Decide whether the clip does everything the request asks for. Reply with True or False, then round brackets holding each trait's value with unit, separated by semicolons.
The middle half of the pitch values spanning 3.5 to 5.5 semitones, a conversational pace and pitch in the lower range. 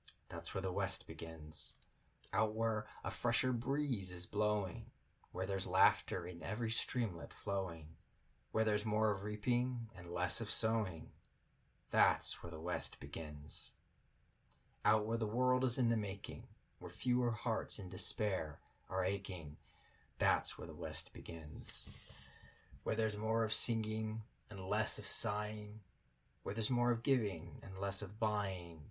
True (3.8 semitones; 145 wpm; 105 Hz)